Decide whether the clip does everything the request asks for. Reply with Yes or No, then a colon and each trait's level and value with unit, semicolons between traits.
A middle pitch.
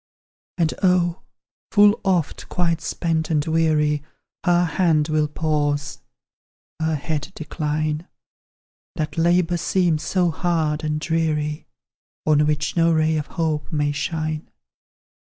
Yes: medium, 160 Hz